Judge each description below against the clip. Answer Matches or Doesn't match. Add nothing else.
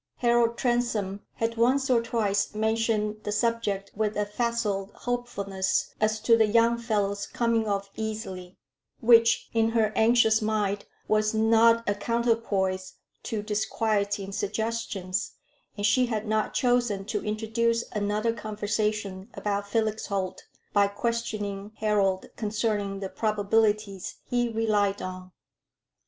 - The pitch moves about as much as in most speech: Doesn't match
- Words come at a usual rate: Doesn't match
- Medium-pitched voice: Doesn't match